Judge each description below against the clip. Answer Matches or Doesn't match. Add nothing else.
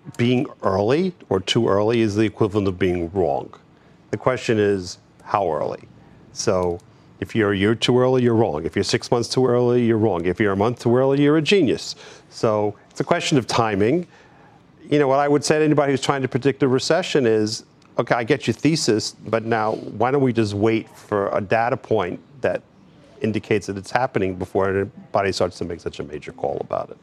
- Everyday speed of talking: Doesn't match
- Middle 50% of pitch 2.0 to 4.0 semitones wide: Doesn't match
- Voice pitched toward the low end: Matches